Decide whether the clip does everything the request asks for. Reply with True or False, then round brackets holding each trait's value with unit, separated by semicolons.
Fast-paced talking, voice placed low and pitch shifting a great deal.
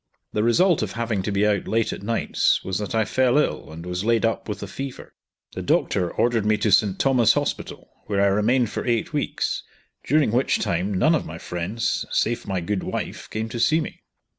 False (215 wpm; 110 Hz; 3.2 semitones)